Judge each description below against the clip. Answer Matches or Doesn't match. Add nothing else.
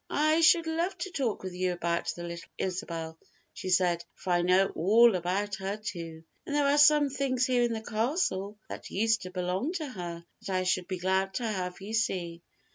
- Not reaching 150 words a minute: Doesn't match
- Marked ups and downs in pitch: Matches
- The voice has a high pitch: Matches